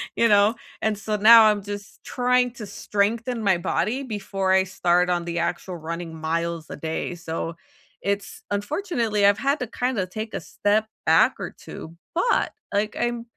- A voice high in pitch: Yes, high, 205 Hz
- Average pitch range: Yes, average, 4.5 semitones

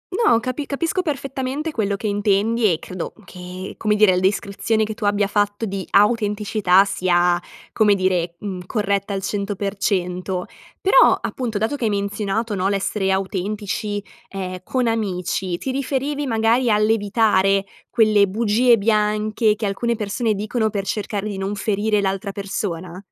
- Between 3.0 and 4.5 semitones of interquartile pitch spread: No, narrow, 2.5 semitones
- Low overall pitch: No, high, 205 Hz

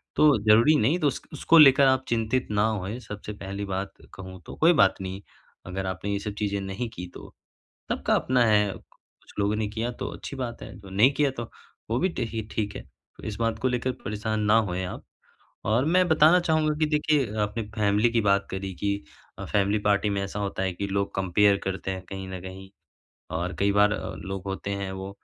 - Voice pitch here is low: Yes, low, 105 Hz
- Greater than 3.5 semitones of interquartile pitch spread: Yes, average, 3.9 semitones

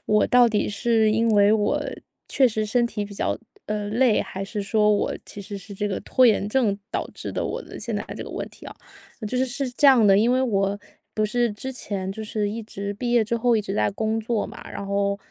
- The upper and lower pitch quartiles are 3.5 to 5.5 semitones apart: No, average, 2.7 semitones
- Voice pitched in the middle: No, high, 215 Hz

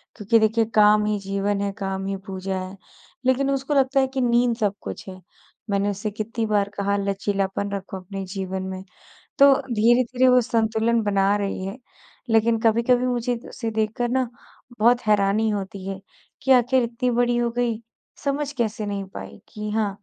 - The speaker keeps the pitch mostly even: No, average, 3.3 semitones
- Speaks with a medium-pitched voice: No, high, 215 Hz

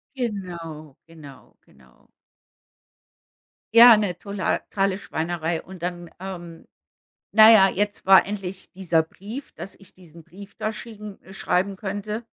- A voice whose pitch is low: No, high, 190 Hz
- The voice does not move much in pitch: No, average, 3.3 semitones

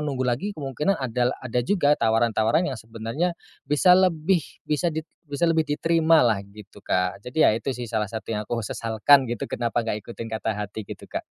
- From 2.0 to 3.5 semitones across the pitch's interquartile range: No, wide, 5.6 semitones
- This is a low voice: Yes, low, 125 Hz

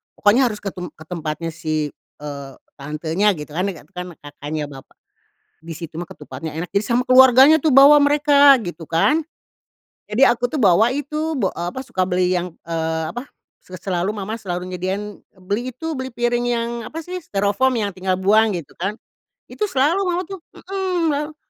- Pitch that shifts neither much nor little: No, wide, 7.5 semitones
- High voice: Yes, high, 205 Hz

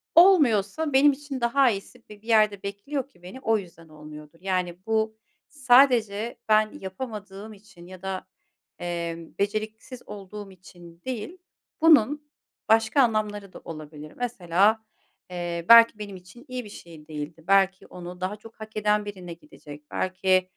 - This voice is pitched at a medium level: No, high, 205 Hz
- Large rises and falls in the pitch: No, average, 4.4 semitones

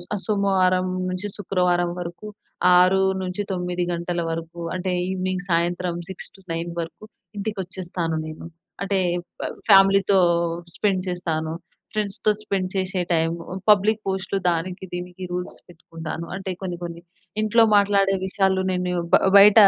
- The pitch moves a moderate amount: No, narrow, 1.9 semitones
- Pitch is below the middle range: No, medium, 185 Hz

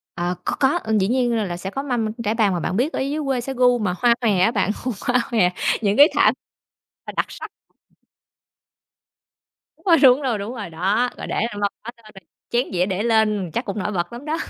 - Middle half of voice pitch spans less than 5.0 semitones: Yes, average, 4.1 semitones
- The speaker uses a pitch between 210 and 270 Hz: Yes, high, 220 Hz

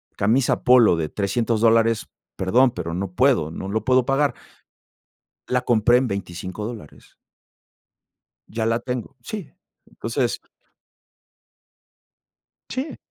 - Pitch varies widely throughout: No, average, 4.2 semitones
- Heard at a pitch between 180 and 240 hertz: No, low, 115 Hz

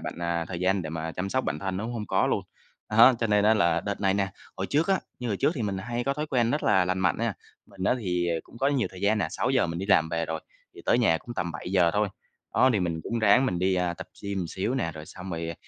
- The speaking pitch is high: No, very low, 95 Hz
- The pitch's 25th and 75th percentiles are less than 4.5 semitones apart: No, average, 4.8 semitones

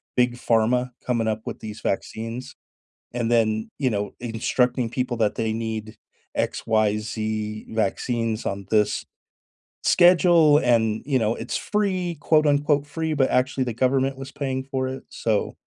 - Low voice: Yes, low, 120 Hz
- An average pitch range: Yes, average, 3.5 semitones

